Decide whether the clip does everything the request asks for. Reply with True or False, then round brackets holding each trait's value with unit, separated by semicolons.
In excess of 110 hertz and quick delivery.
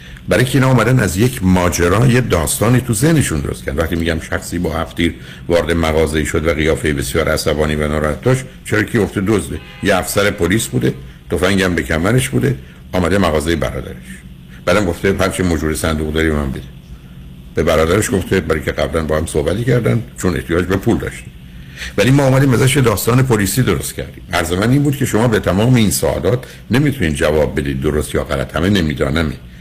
False (85 Hz; 185 wpm)